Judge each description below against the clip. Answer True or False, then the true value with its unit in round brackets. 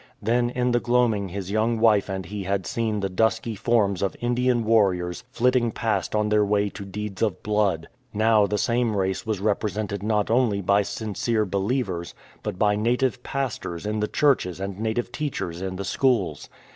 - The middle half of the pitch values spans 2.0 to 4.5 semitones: True (3.1 semitones)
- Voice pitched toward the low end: True (105 Hz)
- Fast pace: False (180 wpm)